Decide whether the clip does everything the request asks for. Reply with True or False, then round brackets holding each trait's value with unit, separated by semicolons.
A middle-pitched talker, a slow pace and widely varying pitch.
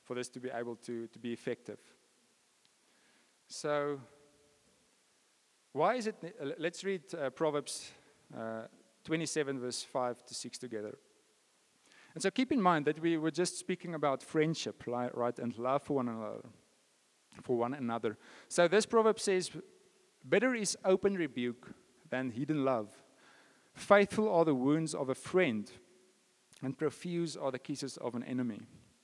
False (145 Hz; 145 wpm; 6.0 semitones)